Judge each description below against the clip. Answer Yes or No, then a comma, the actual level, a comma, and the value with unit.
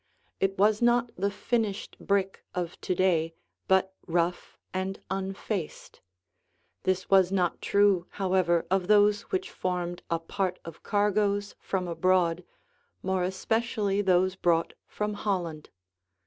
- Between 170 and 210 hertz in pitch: Yes, high, 190 Hz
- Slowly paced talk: Yes, slow, 125 wpm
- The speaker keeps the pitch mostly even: Yes, narrow, 2.3 semitones